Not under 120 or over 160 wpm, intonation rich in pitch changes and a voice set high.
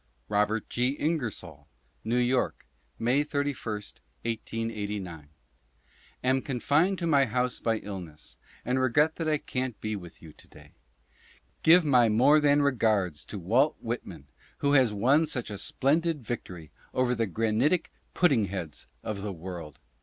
No: average, 150 wpm; wide, 5.9 semitones; low, 120 Hz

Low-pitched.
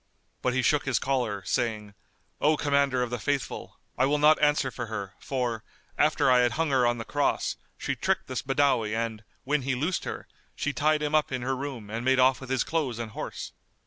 Yes: low, 130 Hz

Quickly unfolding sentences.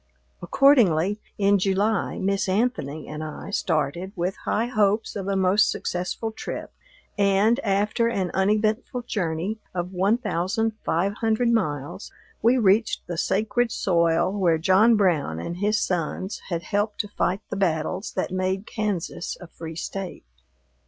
No: average, 145 wpm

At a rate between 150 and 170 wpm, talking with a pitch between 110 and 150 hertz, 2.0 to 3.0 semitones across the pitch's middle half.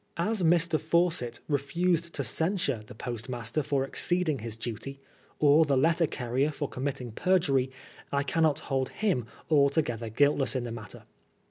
No: average, 155 wpm; medium, 140 Hz; average, 4.7 semitones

